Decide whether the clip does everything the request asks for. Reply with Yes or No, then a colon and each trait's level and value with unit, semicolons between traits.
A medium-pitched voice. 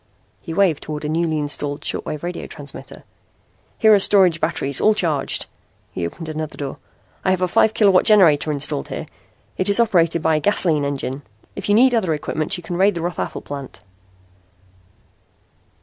Yes: medium, 165 Hz